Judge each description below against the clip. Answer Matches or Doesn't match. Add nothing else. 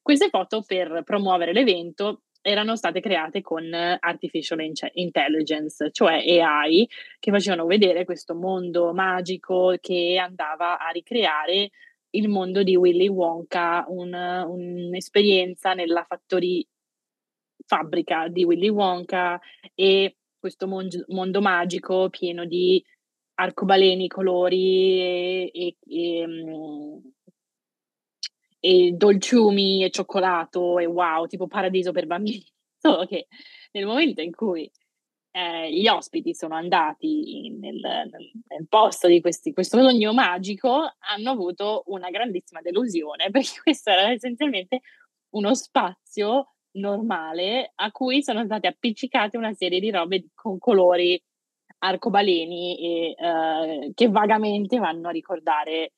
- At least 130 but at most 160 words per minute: Doesn't match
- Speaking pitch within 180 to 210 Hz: Matches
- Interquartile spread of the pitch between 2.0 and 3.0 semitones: Doesn't match